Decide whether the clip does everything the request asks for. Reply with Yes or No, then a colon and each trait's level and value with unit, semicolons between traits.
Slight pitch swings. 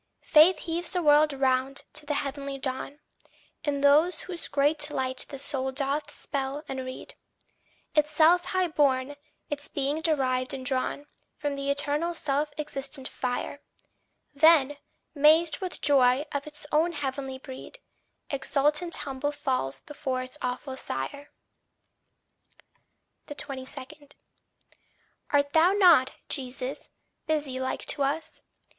Yes: narrow, 2.3 semitones